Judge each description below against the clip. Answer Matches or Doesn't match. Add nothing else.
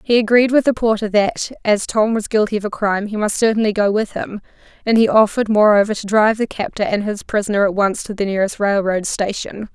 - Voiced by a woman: Matches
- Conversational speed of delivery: Doesn't match